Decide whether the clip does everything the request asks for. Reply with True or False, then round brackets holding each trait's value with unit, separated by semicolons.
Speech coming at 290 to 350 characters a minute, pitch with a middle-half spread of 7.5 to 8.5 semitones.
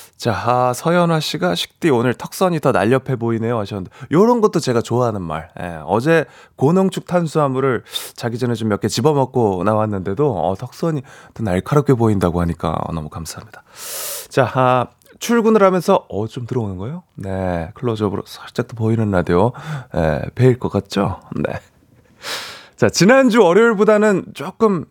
True (335 characters per minute; 7.9 semitones)